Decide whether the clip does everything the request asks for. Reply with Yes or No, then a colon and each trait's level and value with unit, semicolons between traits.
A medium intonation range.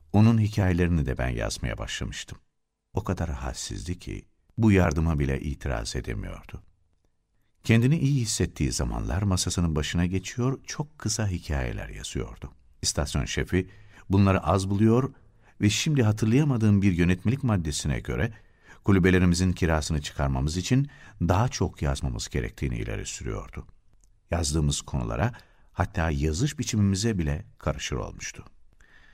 Yes: average, 5.0 semitones